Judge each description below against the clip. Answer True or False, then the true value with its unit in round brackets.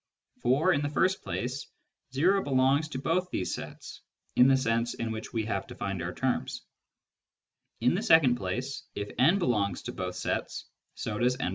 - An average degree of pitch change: True (5.0 semitones)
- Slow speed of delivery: False (175 wpm)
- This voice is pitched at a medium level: False (130 Hz)